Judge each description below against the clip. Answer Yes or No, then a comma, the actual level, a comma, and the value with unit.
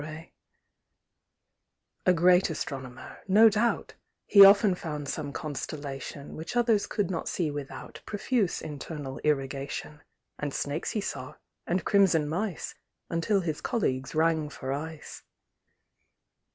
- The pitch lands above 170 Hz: No, medium, 160 Hz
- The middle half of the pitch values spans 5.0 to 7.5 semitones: Yes, average, 5.3 semitones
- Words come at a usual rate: No, slow, 115 wpm